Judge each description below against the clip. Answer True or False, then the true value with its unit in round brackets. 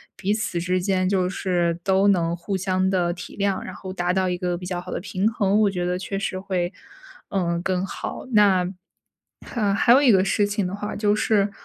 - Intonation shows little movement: True (2.0 semitones)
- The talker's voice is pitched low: False (190 Hz)